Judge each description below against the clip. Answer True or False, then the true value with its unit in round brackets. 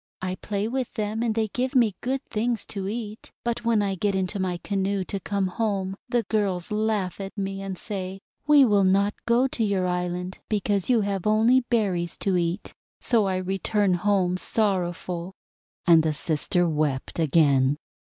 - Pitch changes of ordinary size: True (3.1 semitones)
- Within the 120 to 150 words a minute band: False (175 wpm)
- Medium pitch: False (195 Hz)